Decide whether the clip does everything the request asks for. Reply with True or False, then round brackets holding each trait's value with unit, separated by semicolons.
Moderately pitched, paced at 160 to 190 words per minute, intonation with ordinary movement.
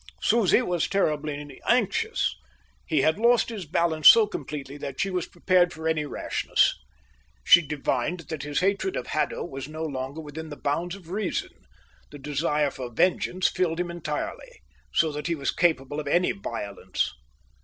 True (160 Hz; 165 wpm; 3.8 semitones)